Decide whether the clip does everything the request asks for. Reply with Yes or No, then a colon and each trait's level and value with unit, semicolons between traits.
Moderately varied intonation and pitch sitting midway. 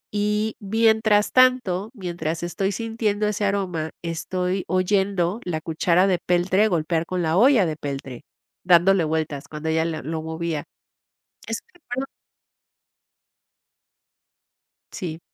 Yes: average, 4.1 semitones; medium, 180 Hz